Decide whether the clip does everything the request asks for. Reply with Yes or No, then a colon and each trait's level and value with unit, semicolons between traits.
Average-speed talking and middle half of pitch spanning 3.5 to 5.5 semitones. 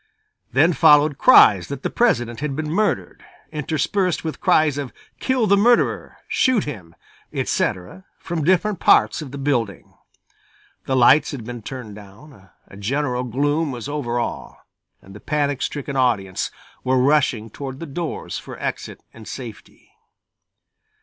Yes: average, 145 wpm; average, 4.7 semitones